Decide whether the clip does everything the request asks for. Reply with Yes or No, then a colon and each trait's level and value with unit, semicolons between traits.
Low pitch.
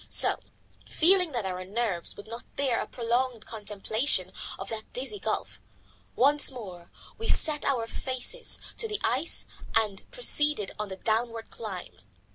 No: high, 230 Hz